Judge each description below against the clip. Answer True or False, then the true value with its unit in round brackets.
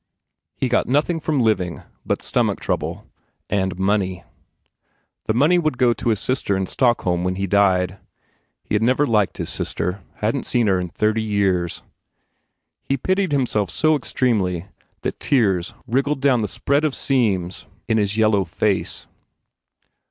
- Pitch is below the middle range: True (110 Hz)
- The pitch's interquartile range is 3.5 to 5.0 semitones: False (5.4 semitones)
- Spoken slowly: False (155 wpm)